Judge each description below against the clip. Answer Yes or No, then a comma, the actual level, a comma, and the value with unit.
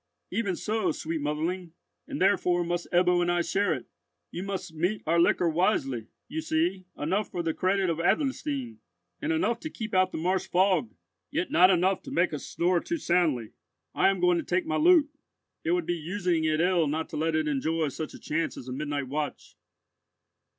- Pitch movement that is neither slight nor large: Yes, average, 3.5 semitones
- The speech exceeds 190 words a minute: Yes, average, 200 wpm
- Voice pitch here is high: No, medium, 175 Hz